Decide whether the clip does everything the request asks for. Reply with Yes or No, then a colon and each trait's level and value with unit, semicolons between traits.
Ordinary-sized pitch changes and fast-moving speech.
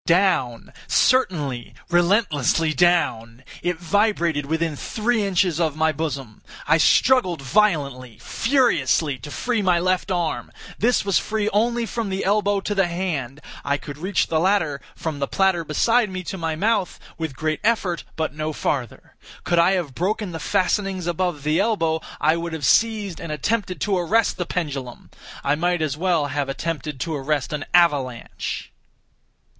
No: average, 4.7 semitones; average, 160 wpm